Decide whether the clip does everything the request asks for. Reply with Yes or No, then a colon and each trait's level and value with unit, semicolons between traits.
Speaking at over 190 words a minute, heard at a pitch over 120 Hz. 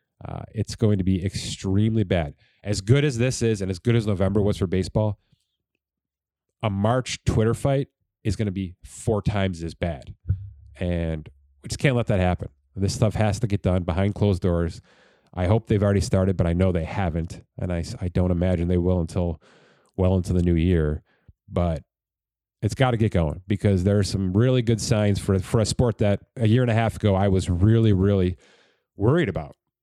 No: fast, 205 wpm; low, 100 Hz